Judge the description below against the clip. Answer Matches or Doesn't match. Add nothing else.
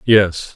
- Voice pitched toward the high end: Doesn't match